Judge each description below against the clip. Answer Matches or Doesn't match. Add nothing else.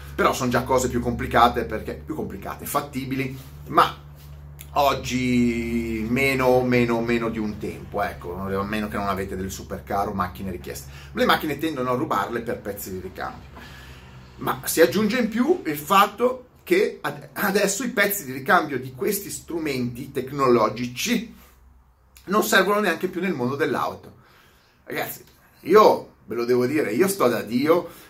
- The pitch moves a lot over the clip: Matches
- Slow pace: Doesn't match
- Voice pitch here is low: Matches